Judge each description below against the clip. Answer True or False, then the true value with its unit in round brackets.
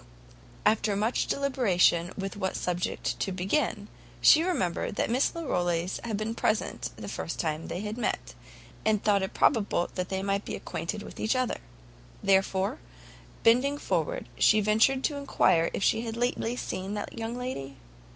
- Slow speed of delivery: False (160 wpm)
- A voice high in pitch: True (210 Hz)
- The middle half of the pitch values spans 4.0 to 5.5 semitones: True (4.4 semitones)